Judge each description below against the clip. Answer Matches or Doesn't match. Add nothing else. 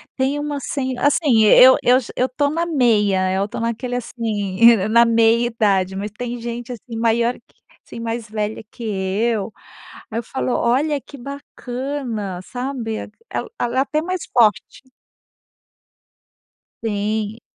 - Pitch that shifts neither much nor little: Matches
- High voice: Matches